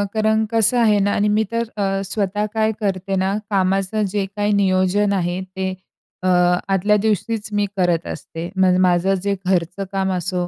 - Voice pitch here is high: Yes, high, 195 Hz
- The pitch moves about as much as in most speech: No, narrow, 2.1 semitones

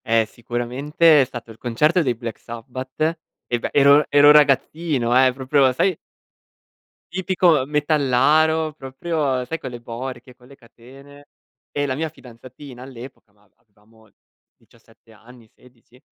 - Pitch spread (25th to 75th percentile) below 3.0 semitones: No, average, 3.6 semitones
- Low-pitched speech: Yes, low, 130 Hz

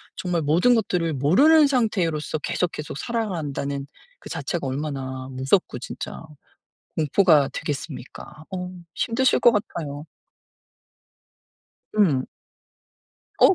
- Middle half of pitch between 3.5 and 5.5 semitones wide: No, wide, 6.1 semitones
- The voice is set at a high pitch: No, medium, 160 Hz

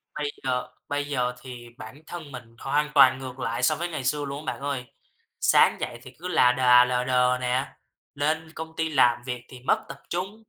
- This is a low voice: Yes, low, 130 Hz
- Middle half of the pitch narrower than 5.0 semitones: Yes, average, 3.1 semitones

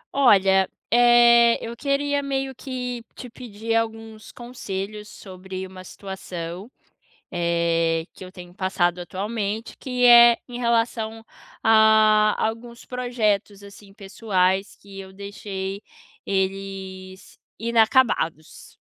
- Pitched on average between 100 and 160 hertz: No, high, 210 Hz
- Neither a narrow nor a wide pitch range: Yes, average, 3.7 semitones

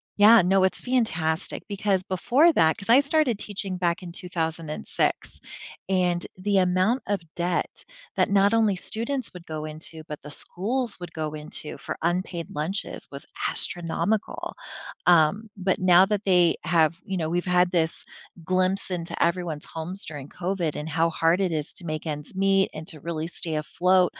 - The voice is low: No, medium, 180 Hz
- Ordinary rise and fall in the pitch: Yes, average, 3.3 semitones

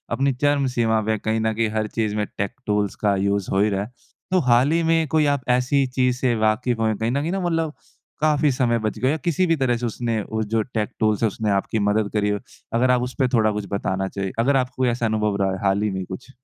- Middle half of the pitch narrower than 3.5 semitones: No, average, 3.8 semitones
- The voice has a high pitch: No, low, 115 Hz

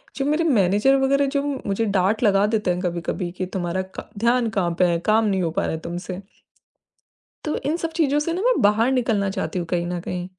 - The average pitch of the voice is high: Yes, high, 205 Hz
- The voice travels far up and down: Yes, wide, 6.6 semitones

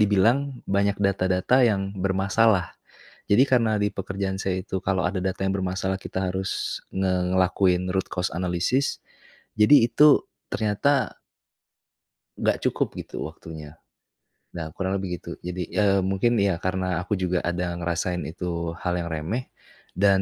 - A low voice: Yes, very low, 95 Hz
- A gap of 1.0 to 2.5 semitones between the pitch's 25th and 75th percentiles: Yes, narrow, 2.1 semitones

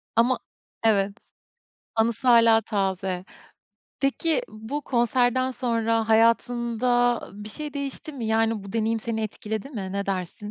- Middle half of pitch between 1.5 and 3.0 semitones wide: Yes, narrow, 2.4 semitones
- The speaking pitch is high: Yes, high, 225 Hz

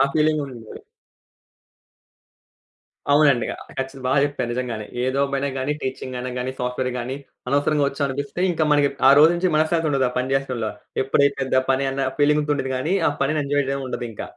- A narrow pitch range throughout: Yes, narrow, 2.1 semitones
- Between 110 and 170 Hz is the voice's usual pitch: Yes, low, 135 Hz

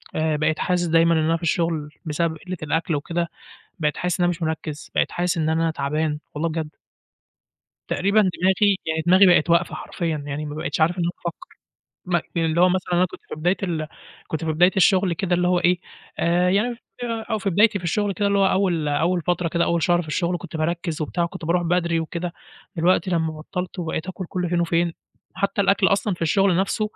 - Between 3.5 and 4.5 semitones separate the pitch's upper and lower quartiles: No, narrow, 2.4 semitones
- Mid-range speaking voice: Yes, medium, 170 Hz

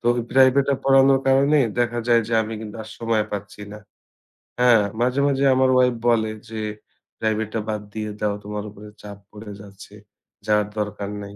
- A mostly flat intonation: No, average, 3.3 semitones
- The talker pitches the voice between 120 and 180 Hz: No, low, 110 Hz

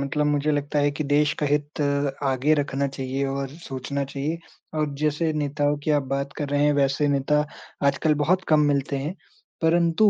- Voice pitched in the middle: Yes, medium, 145 Hz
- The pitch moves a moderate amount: No, narrow, 1.4 semitones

